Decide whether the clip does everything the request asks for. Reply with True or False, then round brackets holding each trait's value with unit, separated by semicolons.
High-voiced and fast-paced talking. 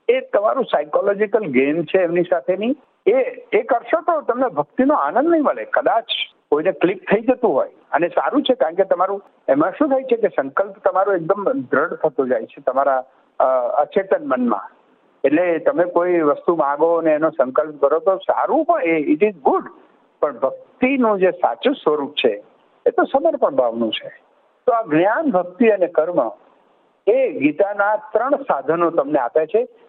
True (210 Hz; 165 wpm)